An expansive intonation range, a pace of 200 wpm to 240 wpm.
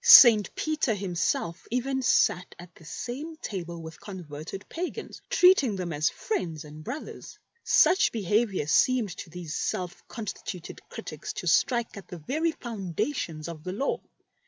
No: wide, 7.0 semitones; average, 155 wpm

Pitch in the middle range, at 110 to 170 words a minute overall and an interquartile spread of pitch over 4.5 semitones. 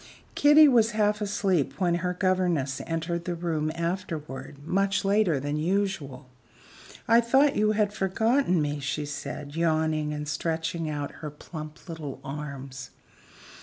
Yes: medium, 165 Hz; slow, 135 wpm; average, 4.9 semitones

